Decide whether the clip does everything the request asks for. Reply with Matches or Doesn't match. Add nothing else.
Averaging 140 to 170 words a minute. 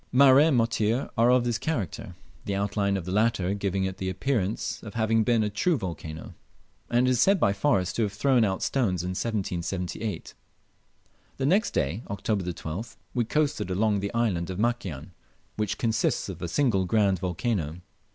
Doesn't match